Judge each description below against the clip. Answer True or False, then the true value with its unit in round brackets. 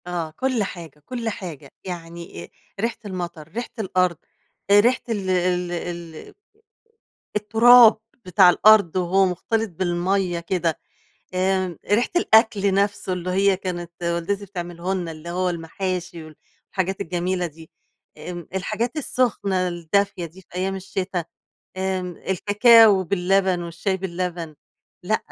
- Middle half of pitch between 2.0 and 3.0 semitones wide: True (2.5 semitones)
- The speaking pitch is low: False (185 Hz)